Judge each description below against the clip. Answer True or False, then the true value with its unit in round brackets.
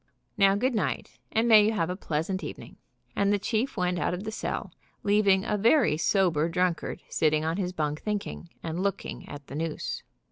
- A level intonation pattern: False (4.1 semitones)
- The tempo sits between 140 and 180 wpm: False (190 wpm)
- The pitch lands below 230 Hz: True (190 Hz)